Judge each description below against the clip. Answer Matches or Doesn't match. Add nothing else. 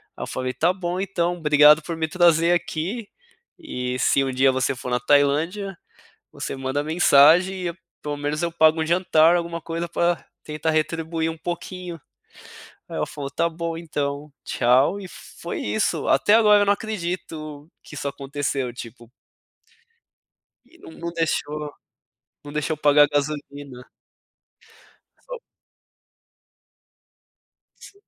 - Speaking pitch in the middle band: Matches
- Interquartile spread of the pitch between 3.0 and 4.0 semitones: Matches